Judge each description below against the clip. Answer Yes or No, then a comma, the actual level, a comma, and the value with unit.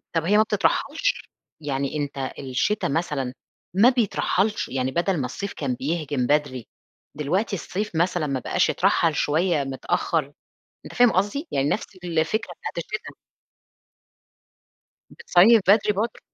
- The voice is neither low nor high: Yes, medium, 170 Hz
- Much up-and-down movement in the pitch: Yes, wide, 6.6 semitones